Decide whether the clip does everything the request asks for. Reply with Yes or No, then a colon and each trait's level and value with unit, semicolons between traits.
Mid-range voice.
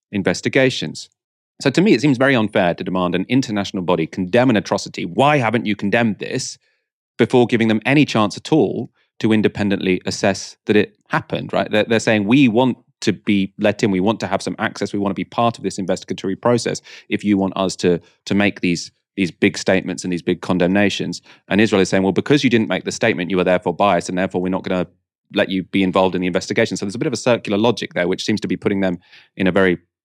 No: low, 100 Hz